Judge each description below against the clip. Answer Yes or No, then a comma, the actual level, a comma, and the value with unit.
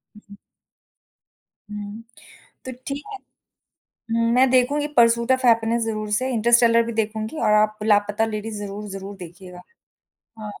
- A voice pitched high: Yes, high, 220 Hz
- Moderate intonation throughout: No, narrow, 2.1 semitones